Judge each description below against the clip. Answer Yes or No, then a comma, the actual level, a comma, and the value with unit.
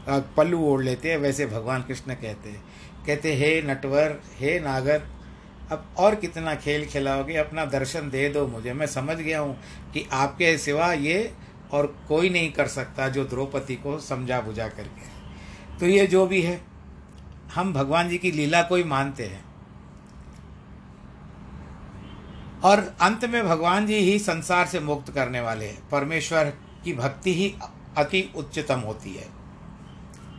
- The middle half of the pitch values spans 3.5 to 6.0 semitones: Yes, average, 5.0 semitones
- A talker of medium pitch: Yes, medium, 145 Hz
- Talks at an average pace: Yes, average, 150 wpm